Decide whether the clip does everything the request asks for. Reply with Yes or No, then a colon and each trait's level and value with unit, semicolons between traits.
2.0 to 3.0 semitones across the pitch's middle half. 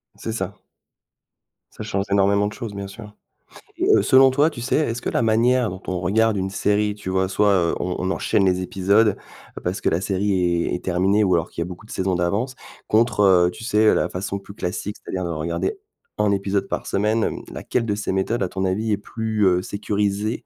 Yes: average, 2.7 semitones